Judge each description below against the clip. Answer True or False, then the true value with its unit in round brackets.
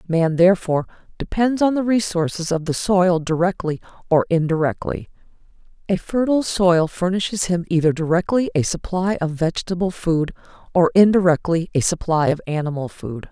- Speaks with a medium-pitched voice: True (175 Hz)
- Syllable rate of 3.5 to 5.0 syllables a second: False (5.3 syllables/s)